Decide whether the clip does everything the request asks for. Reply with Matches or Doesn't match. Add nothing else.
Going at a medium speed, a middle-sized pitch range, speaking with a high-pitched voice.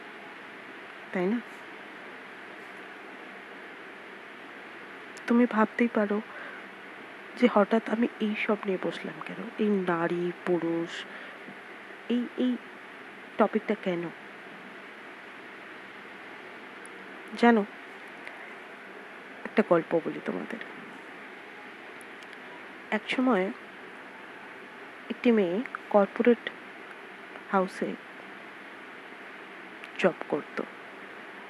Matches